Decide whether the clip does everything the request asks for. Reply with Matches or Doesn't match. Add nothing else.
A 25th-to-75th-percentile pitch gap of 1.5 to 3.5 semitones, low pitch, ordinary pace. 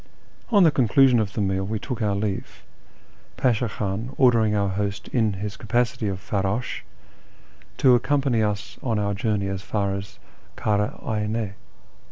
Matches